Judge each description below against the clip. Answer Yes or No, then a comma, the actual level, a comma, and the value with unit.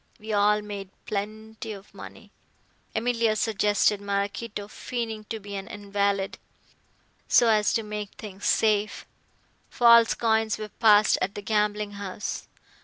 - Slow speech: Yes, slow, 130 wpm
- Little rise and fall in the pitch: Yes, narrow, 1.5 semitones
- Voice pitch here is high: Yes, high, 210 Hz